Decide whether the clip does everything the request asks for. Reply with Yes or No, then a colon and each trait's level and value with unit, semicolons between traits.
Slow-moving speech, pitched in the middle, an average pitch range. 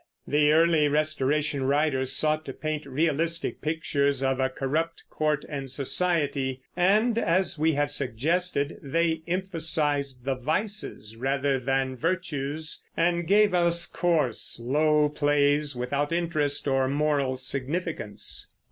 Yes: slow, 120 wpm; medium, 150 Hz; average, 3.4 semitones